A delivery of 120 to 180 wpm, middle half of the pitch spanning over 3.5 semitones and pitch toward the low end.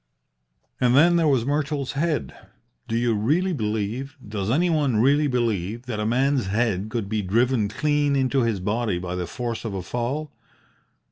Yes: average, 165 wpm; average, 5.0 semitones; low, 120 Hz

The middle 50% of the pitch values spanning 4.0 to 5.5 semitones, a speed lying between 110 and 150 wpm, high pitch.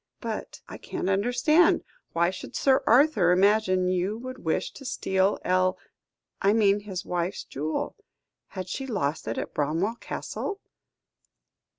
Yes: average, 4.6 semitones; slow, 135 wpm; high, 195 Hz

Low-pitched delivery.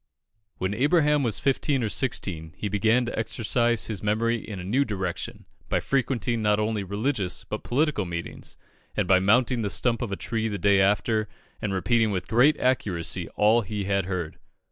Yes: low, 110 Hz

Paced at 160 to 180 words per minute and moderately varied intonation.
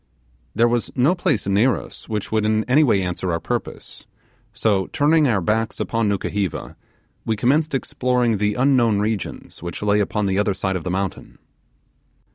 Yes: average, 170 wpm; average, 4.0 semitones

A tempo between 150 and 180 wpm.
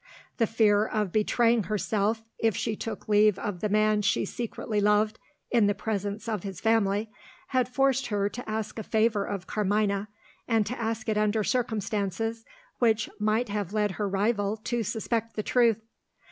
Yes: average, 170 wpm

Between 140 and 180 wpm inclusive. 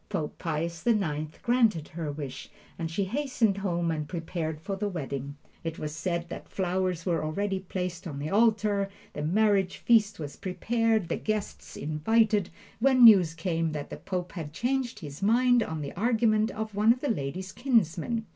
Yes: average, 175 wpm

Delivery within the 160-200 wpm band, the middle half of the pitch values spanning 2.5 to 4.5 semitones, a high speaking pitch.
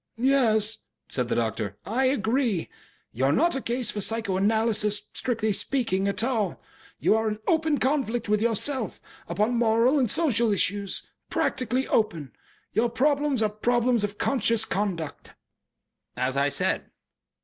No: average, 140 wpm; average, 3.7 semitones; high, 225 Hz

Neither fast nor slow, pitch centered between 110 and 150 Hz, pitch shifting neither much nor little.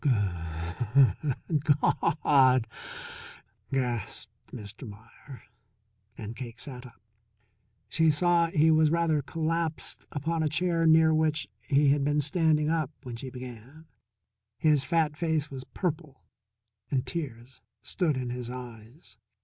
No: slow, 125 wpm; medium, 140 Hz; average, 4.3 semitones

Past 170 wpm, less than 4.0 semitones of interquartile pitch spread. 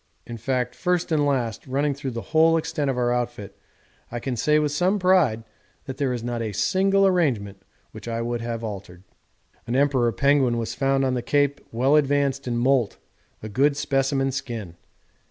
Yes: average, 190 wpm; average, 3.5 semitones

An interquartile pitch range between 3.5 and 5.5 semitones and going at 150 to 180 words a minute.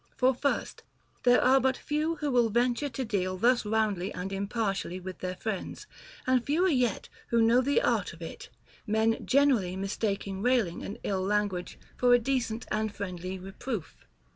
Yes: average, 4.6 semitones; average, 170 wpm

